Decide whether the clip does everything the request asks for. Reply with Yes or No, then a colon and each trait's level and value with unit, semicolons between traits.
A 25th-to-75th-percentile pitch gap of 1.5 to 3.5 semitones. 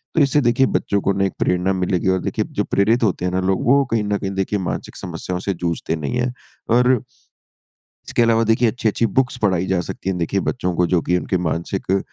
No: average, 4.2 semitones